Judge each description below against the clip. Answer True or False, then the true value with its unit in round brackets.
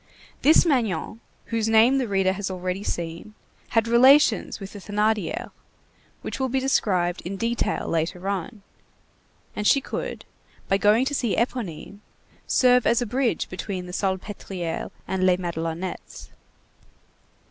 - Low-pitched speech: False (205 Hz)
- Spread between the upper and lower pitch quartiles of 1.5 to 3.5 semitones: False (4.3 semitones)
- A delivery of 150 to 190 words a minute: False (135 wpm)